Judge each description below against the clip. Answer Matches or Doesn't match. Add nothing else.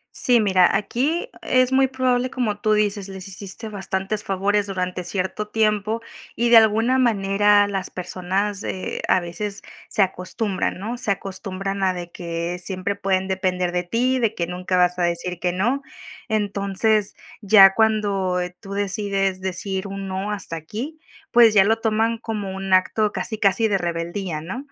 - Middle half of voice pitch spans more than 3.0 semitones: Doesn't match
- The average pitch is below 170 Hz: Doesn't match